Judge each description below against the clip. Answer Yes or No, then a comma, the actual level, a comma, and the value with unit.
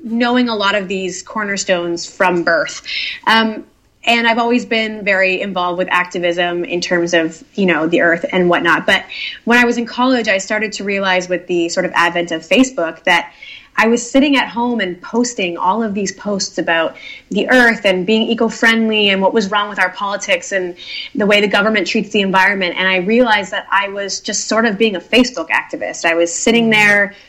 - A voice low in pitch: No, high, 200 Hz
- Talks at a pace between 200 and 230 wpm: Yes, fast, 205 wpm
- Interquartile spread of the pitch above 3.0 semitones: Yes, average, 4.1 semitones